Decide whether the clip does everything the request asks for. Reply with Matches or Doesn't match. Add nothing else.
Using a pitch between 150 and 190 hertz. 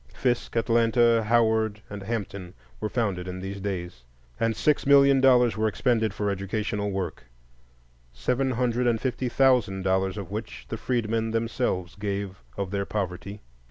Doesn't match